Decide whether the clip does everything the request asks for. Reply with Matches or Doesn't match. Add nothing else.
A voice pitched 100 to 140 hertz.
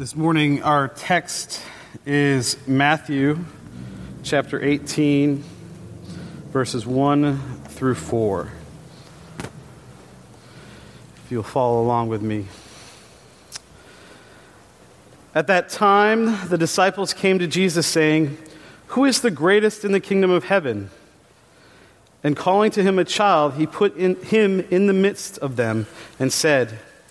Doesn't match